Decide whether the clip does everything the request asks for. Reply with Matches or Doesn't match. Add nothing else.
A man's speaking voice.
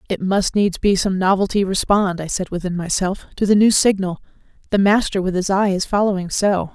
Doesn't match